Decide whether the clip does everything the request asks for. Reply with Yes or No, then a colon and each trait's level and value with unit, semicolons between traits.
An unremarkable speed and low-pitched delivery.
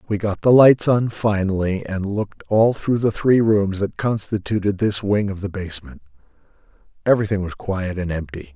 Yes: average, 175 wpm; low, 100 Hz